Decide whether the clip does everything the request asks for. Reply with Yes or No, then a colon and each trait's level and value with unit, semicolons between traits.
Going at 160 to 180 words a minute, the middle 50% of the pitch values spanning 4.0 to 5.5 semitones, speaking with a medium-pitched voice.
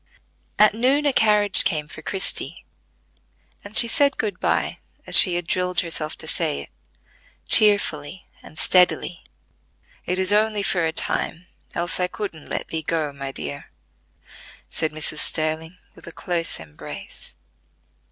No: average, 145 wpm; average, 4.6 semitones; medium, 175 Hz